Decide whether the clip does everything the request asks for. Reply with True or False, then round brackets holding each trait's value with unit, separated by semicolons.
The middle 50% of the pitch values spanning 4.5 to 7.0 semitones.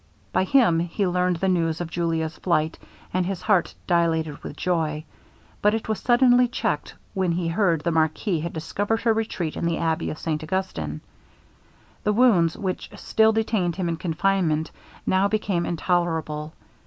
False (3.3 semitones)